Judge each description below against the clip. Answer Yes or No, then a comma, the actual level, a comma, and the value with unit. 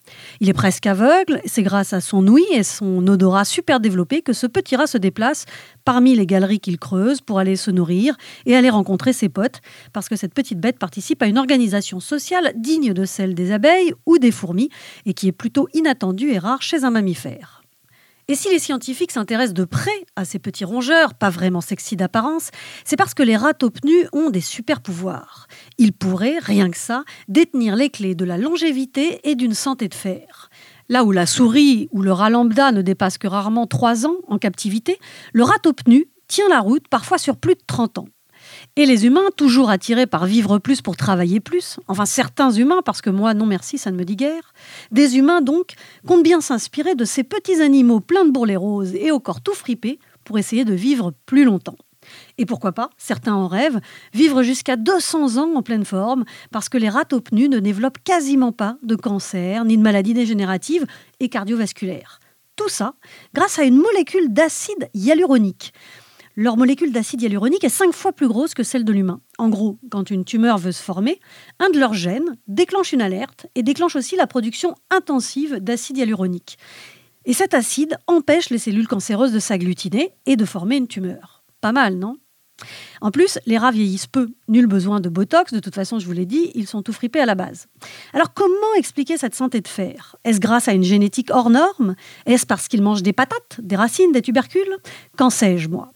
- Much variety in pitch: Yes, wide, 6.2 semitones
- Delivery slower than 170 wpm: No, average, 200 wpm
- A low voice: No, high, 240 Hz